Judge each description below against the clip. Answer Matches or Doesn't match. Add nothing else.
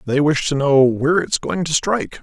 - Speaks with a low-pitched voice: Doesn't match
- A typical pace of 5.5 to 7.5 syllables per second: Matches